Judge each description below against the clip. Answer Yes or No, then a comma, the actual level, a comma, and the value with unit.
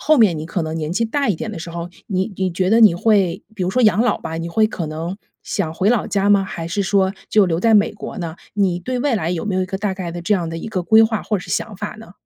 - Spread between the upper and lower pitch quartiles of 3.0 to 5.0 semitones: Yes, average, 3.9 semitones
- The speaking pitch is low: No, high, 190 Hz